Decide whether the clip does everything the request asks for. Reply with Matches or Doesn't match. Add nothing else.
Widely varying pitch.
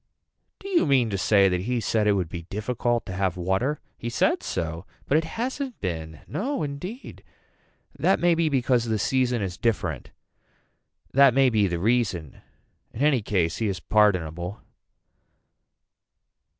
Matches